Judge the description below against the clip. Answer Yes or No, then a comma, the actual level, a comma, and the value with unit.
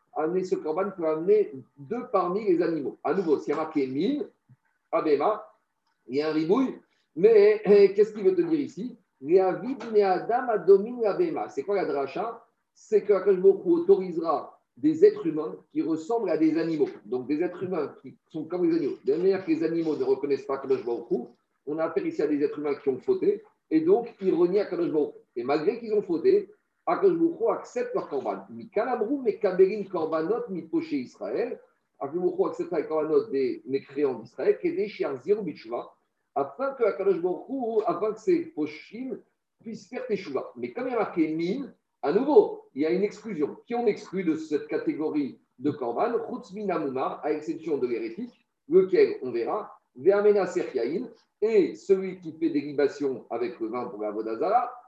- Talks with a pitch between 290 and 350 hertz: Yes, very high, 310 Hz